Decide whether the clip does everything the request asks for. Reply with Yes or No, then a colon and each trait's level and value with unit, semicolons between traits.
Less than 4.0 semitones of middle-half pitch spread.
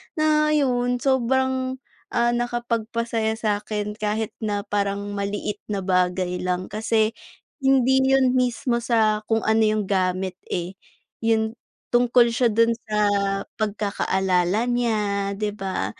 Yes: average, 3.1 semitones